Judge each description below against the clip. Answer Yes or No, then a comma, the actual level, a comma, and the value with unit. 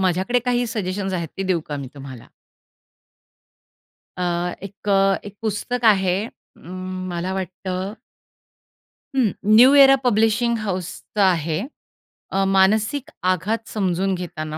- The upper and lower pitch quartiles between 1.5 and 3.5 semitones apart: Yes, average, 3.2 semitones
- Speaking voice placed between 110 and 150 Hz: No, high, 190 Hz